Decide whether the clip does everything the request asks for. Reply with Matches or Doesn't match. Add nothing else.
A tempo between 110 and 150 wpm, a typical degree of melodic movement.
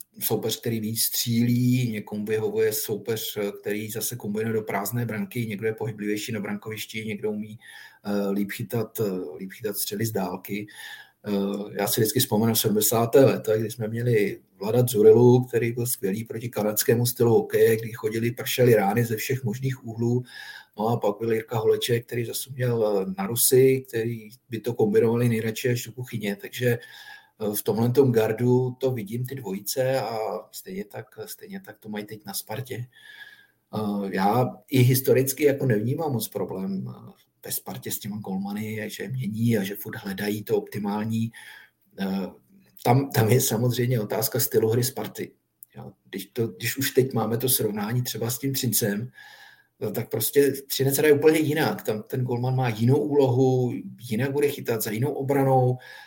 Doesn't match